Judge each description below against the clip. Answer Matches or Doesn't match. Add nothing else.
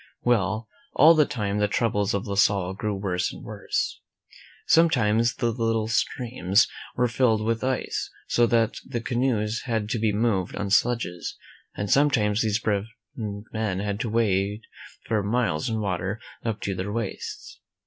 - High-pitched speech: Doesn't match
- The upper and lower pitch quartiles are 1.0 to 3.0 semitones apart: Matches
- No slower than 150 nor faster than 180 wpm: Matches